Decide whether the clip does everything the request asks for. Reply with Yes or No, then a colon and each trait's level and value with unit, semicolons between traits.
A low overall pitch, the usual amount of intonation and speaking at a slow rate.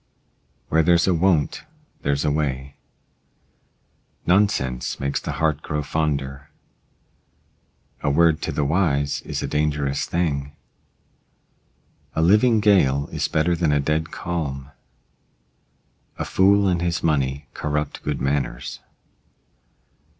Yes: very low, 75 Hz; average, 3.4 semitones; slow, 115 wpm